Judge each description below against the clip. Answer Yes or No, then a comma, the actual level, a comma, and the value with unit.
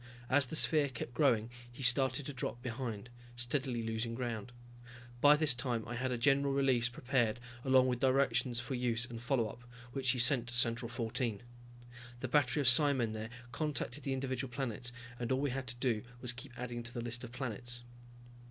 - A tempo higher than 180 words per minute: Yes, average, 190 wpm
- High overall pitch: No, low, 125 Hz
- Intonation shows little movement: Yes, narrow, 2.0 semitones